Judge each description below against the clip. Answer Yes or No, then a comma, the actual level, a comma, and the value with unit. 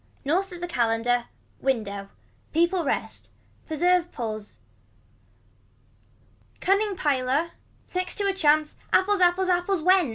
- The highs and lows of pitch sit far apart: Yes, wide, 6.2 semitones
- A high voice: Yes, very high, 340 Hz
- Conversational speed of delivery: No, slow, 110 wpm